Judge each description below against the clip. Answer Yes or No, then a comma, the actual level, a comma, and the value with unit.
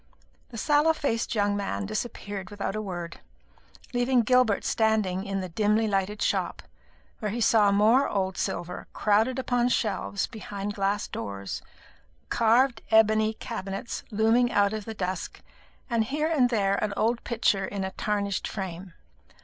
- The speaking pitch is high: Yes, high, 210 Hz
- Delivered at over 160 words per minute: No, average, 150 wpm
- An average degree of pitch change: Yes, average, 3.0 semitones